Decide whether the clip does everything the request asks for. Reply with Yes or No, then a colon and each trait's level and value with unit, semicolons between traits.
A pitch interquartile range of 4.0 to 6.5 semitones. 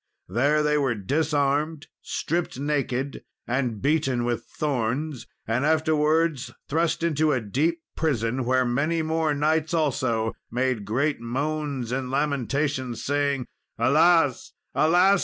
No: average, 3.6 semitones